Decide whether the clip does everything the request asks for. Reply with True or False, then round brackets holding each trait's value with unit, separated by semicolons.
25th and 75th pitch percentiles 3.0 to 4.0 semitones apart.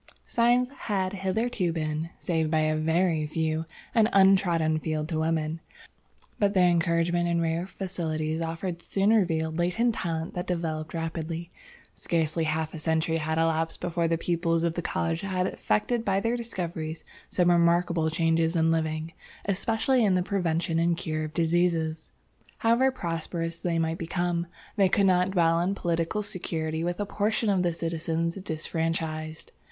False (2.4 semitones)